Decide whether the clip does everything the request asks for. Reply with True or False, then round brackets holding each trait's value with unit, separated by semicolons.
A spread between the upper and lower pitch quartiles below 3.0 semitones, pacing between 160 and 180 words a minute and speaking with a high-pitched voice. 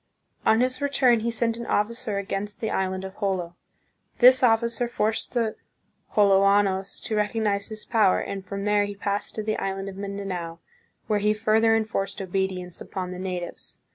True (2.5 semitones; 170 wpm; 205 Hz)